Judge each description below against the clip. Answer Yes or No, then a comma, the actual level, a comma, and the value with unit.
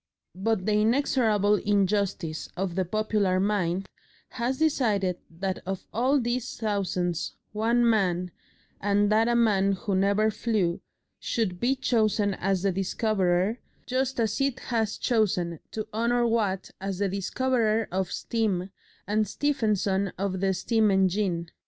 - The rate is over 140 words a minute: No, slow, 135 wpm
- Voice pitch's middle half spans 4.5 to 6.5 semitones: No, average, 3.1 semitones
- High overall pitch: Yes, high, 205 Hz